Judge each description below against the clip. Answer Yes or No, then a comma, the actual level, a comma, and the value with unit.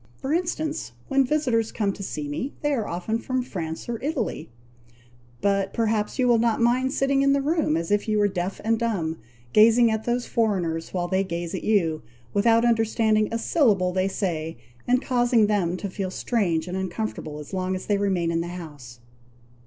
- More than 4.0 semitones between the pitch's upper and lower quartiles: Yes, average, 4.9 semitones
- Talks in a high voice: Yes, high, 210 Hz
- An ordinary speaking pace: Yes, average, 190 wpm